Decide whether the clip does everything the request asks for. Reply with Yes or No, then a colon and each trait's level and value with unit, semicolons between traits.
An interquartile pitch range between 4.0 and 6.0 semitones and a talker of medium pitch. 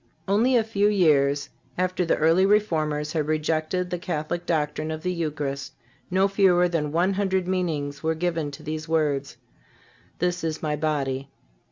No: average, 3.3 semitones; medium, 160 Hz